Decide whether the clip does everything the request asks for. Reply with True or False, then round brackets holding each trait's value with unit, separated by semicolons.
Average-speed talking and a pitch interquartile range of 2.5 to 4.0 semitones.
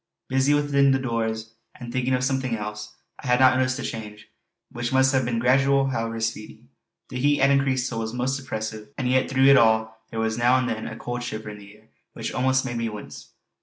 False (225 wpm; 2.9 semitones)